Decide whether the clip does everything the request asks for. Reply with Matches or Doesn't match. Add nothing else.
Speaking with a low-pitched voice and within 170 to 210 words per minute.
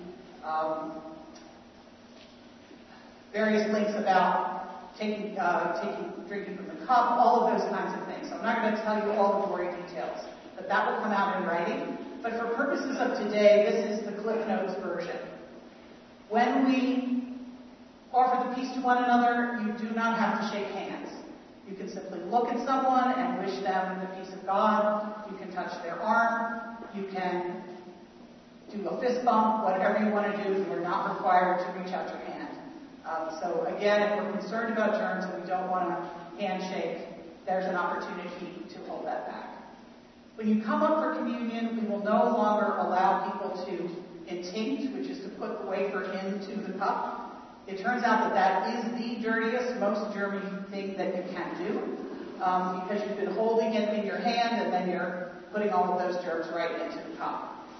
Doesn't match